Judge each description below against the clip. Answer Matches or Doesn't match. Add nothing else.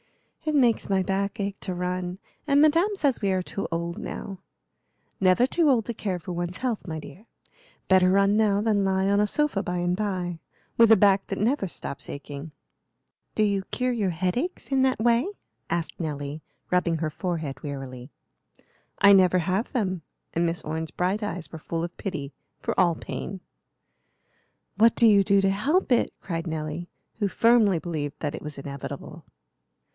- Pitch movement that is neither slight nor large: Matches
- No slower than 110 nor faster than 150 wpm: Doesn't match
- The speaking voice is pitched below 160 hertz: Doesn't match